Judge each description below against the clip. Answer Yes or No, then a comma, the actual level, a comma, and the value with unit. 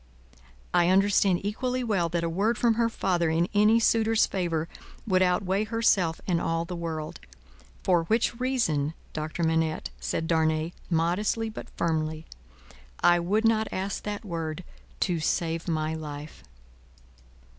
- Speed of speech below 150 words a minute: Yes, average, 140 wpm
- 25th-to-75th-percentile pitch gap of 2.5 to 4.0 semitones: No, average, 4.5 semitones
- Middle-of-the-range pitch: Yes, medium, 175 Hz